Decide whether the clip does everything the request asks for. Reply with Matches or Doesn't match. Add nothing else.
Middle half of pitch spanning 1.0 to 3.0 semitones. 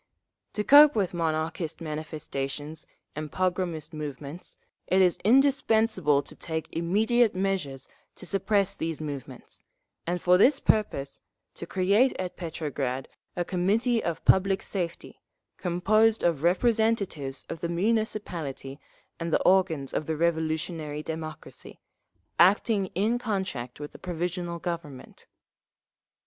Doesn't match